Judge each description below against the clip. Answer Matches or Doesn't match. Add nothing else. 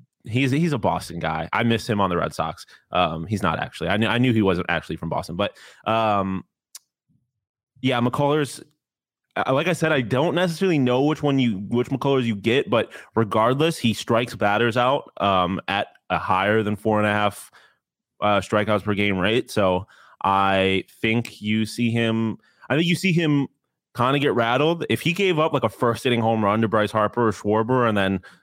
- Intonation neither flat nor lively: Matches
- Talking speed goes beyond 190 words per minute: Matches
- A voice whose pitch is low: Matches